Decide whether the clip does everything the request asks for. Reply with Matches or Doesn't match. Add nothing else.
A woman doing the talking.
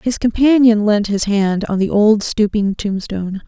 Matches